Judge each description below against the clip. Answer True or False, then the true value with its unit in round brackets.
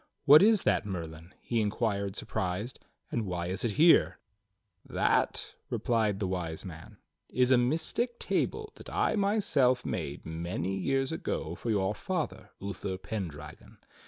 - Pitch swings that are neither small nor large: False (6.5 semitones)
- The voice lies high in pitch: False (105 Hz)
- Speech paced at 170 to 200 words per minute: False (140 wpm)